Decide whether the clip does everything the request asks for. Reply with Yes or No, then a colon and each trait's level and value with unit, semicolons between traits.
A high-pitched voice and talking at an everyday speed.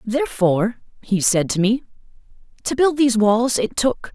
Yes: high, 230 Hz; average, 160 wpm